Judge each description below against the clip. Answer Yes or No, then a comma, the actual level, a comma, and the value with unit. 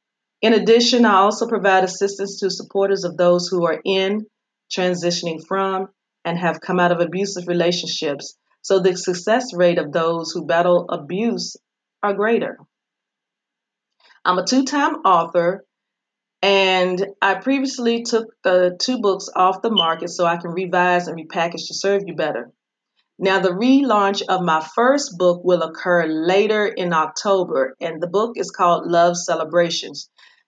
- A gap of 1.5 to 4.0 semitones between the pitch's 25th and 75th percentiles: Yes, average, 3.0 semitones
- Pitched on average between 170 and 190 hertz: Yes, medium, 185 Hz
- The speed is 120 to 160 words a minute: Yes, average, 150 wpm